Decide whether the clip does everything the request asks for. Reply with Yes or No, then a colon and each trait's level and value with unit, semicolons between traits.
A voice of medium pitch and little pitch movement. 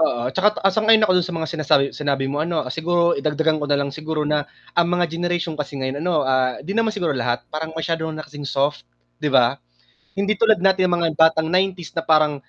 No: medium, 160 Hz; average, 3.2 semitones